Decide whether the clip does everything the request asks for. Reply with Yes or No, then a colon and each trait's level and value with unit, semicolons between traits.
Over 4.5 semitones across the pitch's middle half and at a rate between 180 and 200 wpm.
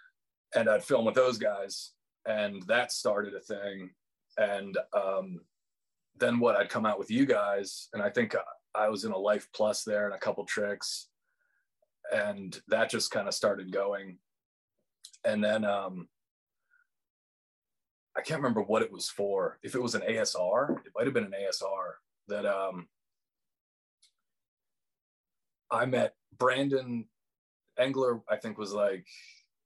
No: average, 5.3 semitones; average, 150 wpm